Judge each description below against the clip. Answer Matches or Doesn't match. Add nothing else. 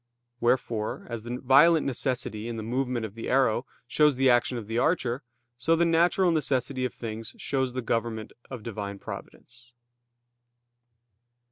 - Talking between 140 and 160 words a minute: Matches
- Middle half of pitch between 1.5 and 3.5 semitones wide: Matches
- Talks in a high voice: Doesn't match